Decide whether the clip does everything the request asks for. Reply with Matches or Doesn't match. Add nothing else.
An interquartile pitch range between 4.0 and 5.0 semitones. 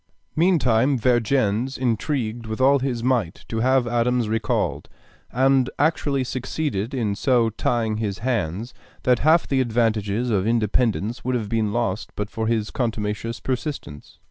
Doesn't match